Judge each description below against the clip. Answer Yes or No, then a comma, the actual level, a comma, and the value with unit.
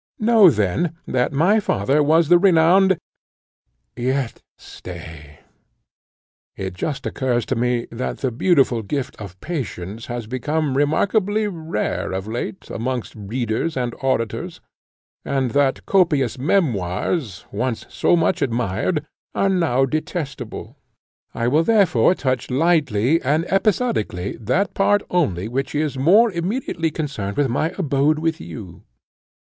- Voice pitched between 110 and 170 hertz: Yes, low, 135 Hz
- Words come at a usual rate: No, slow, 125 wpm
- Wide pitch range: Yes, wide, 6.4 semitones